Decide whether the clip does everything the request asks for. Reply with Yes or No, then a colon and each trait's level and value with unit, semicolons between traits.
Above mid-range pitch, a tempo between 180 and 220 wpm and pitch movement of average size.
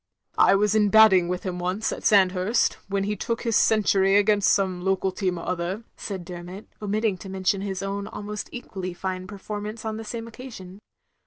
No: high, 195 Hz; average, 195 wpm; narrow, 2.3 semitones